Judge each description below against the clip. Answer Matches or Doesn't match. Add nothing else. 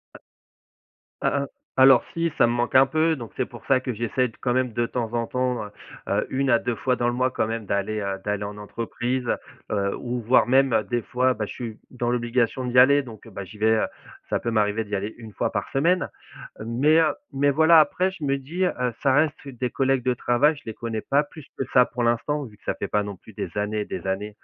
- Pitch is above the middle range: Doesn't match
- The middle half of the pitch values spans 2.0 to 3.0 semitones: Doesn't match